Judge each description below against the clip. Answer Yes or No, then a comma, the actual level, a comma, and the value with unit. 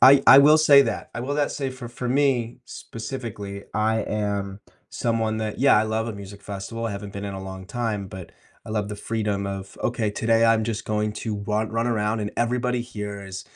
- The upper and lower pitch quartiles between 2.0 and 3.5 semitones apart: Yes, average, 2.7 semitones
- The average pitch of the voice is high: No, low, 110 Hz